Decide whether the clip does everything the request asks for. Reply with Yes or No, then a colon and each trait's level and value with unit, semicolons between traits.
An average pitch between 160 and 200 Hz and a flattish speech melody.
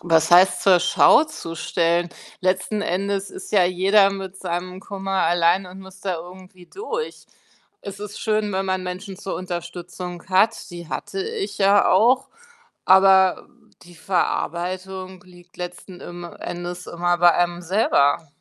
Yes: medium, 185 Hz; narrow, 1.8 semitones